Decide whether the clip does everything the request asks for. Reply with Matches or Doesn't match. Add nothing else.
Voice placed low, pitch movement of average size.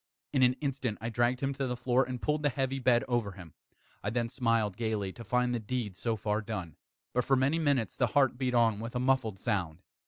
Matches